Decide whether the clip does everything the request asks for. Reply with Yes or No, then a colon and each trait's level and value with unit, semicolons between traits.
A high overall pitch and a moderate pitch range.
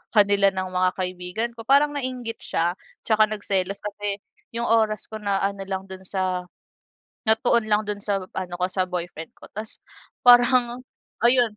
Yes: high, 205 Hz; average, 3.4 semitones